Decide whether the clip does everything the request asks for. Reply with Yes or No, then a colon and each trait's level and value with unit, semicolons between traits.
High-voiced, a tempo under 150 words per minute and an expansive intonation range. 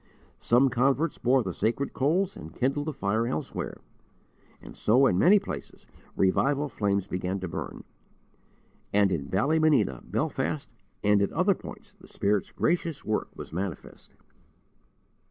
No: low, 120 Hz; slow, 135 wpm; wide, 6.6 semitones